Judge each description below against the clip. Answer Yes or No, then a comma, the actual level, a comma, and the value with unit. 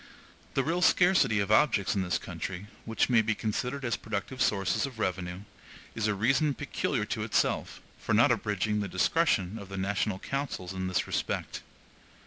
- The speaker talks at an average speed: Yes, average, 170 wpm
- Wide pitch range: No, average, 5.0 semitones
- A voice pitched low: Yes, low, 105 Hz